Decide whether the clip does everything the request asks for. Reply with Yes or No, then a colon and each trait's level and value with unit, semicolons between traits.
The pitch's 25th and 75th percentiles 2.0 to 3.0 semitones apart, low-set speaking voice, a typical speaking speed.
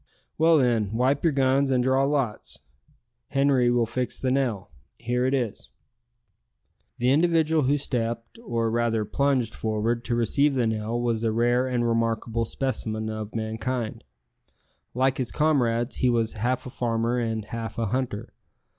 Yes: narrow, 2.6 semitones; low, 120 Hz; average, 155 wpm